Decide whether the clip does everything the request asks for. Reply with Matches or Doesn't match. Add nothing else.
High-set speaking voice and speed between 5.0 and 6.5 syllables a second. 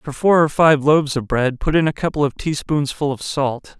Doesn't match